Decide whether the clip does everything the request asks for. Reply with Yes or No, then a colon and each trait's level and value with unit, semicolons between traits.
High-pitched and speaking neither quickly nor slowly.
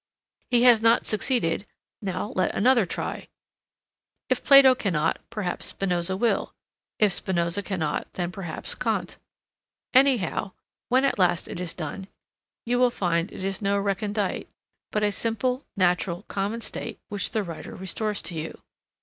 Yes: high, 200 Hz; average, 145 wpm